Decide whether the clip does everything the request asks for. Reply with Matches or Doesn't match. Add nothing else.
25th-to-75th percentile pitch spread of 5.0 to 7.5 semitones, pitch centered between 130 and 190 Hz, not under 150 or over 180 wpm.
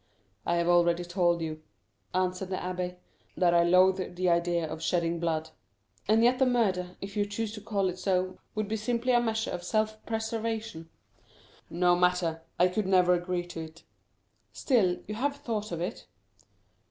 Doesn't match